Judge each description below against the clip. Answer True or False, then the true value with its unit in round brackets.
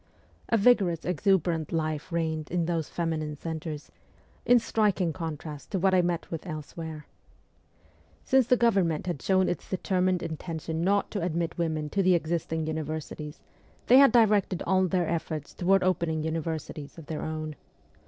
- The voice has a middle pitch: True (170 Hz)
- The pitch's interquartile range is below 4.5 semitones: True (2.9 semitones)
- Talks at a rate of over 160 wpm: False (155 wpm)